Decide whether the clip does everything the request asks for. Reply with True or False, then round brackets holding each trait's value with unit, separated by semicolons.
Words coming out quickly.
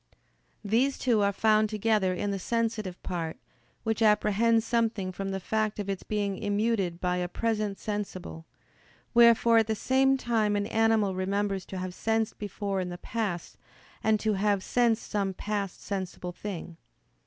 False (160 wpm)